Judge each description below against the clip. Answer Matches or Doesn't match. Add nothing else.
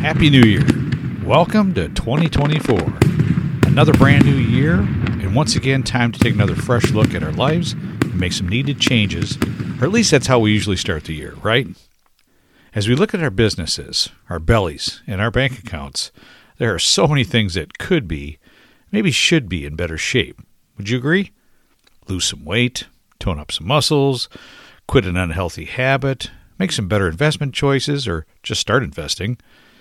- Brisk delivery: Doesn't match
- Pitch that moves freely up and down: Matches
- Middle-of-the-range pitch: Doesn't match